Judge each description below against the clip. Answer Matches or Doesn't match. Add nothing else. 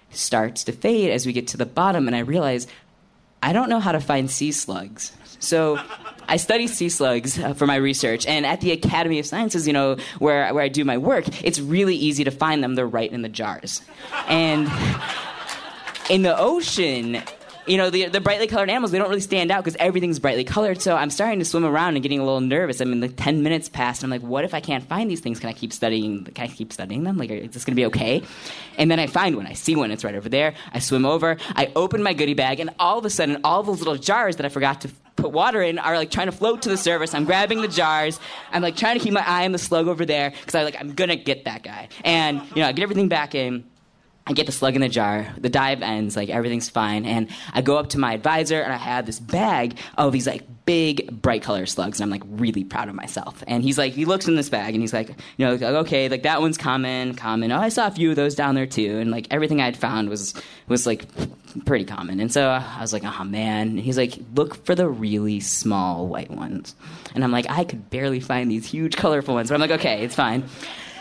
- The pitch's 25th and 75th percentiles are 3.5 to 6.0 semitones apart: Matches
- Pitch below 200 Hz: Matches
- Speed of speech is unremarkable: Doesn't match